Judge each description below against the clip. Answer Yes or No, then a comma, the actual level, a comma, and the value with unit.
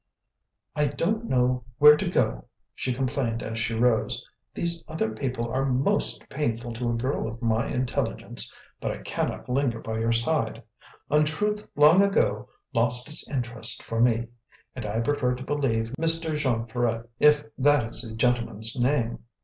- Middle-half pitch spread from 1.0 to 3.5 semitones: No, average, 4.2 semitones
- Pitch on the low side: Yes, low, 125 Hz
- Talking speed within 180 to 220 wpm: No, average, 160 wpm